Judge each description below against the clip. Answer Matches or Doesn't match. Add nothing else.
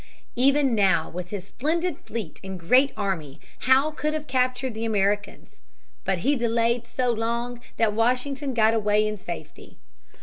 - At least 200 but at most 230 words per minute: Doesn't match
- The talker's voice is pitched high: Matches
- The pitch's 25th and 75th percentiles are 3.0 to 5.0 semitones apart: Matches